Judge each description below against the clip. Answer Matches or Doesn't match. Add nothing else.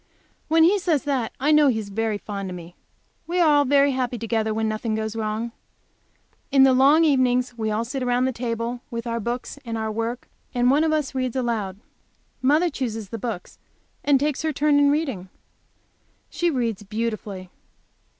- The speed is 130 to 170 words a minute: Doesn't match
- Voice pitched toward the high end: Matches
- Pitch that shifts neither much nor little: Matches